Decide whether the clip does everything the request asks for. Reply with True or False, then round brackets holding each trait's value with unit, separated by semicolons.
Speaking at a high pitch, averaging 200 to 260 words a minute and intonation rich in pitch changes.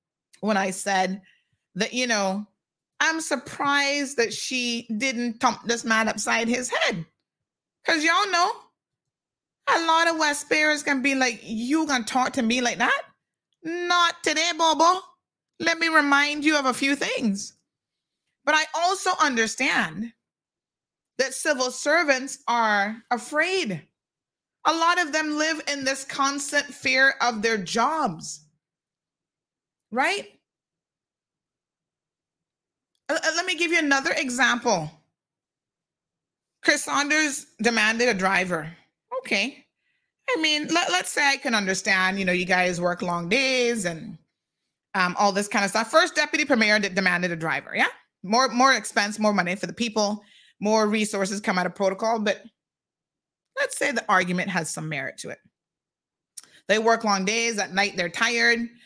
False (240 Hz; 145 wpm; 6.5 semitones)